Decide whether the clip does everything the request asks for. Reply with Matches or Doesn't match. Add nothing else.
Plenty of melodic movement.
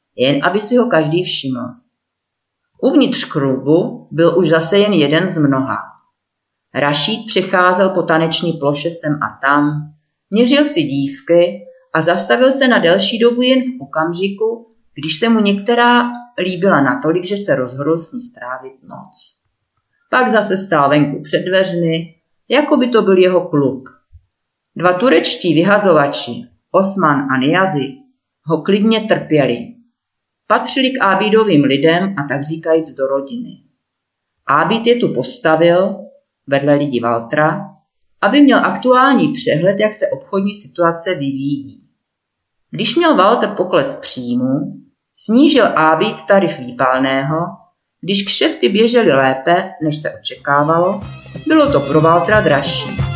Matches